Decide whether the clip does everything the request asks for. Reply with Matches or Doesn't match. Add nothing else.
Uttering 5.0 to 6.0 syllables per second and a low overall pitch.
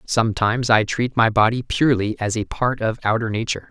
Matches